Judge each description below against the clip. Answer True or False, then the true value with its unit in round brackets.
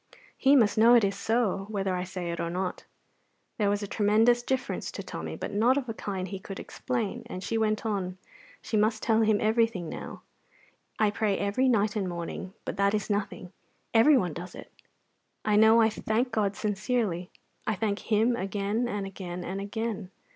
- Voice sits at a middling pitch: False (210 Hz)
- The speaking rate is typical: True (190 wpm)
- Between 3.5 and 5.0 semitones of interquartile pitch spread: False (2.6 semitones)